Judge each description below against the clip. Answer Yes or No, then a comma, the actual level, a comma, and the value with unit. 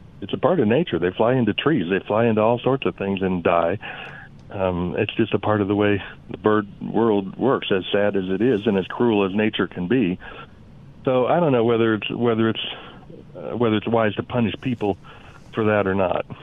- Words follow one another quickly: Yes, fast, 225 wpm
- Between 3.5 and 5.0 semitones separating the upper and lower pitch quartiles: No, average, 2.8 semitones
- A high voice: No, low, 105 Hz